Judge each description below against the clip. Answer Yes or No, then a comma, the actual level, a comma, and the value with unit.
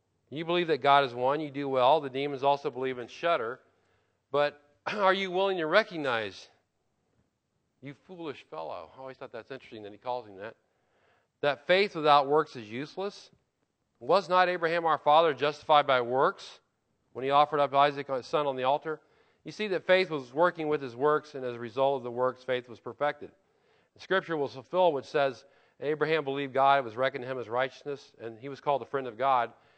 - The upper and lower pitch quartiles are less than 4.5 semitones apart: Yes, average, 3.0 semitones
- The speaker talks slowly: No, fast, 205 wpm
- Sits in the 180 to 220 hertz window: No, medium, 140 Hz